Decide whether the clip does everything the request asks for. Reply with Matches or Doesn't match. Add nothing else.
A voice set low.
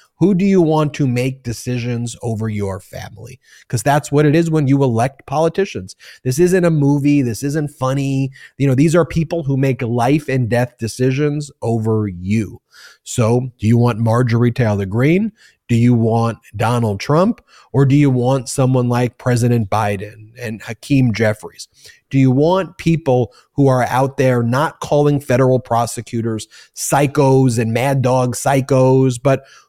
Matches